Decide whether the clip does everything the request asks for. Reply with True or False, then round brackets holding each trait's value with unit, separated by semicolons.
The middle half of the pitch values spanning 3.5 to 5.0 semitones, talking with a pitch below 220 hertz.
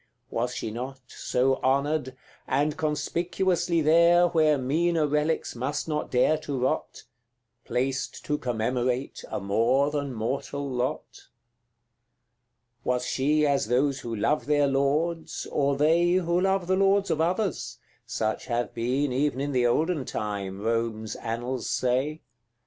True (3.9 semitones; 140 Hz)